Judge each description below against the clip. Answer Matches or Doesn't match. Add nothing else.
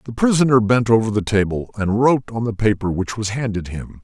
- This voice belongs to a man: Matches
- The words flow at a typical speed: Doesn't match